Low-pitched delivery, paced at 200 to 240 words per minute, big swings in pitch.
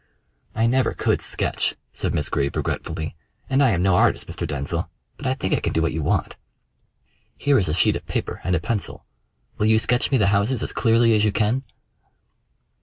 Yes: low, 105 Hz; fast, 205 wpm; wide, 5.7 semitones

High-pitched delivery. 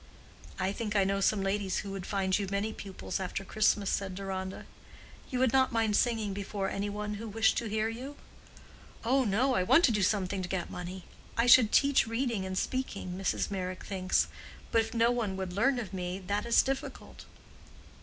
Yes: high, 205 Hz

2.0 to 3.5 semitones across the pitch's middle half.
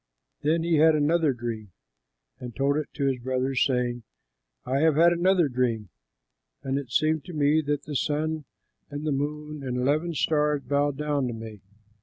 Yes: average, 3.2 semitones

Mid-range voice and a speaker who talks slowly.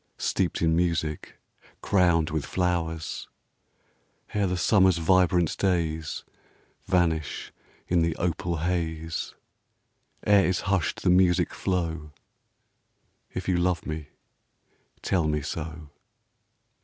No: very low, 85 Hz; slow, 105 wpm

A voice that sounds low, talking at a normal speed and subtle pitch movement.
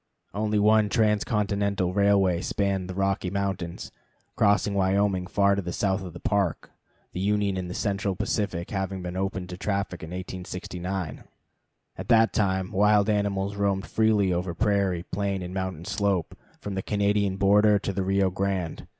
Yes: low, 100 Hz; average, 160 wpm; narrow, 1.7 semitones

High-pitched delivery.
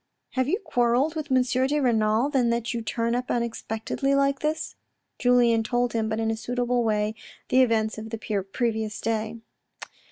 Yes: high, 235 Hz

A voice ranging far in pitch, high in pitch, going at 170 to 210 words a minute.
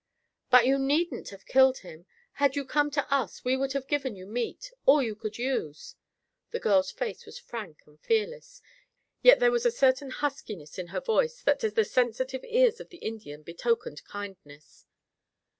Yes: wide, 8.7 semitones; very high, 265 Hz; average, 180 wpm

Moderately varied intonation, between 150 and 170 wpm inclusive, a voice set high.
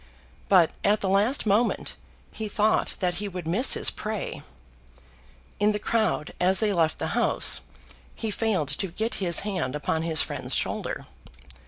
Yes: average, 3.8 semitones; average, 160 wpm; high, 200 Hz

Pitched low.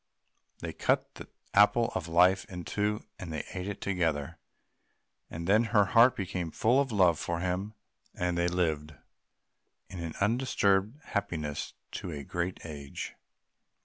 Yes: very low, 90 Hz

